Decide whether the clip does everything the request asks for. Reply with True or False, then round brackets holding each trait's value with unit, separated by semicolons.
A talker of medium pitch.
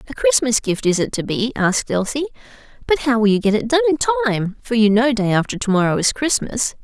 False (240 Hz)